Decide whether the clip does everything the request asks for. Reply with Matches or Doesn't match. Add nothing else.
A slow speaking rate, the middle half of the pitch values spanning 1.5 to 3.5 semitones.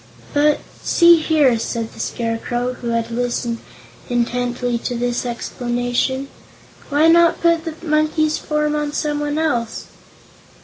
Doesn't match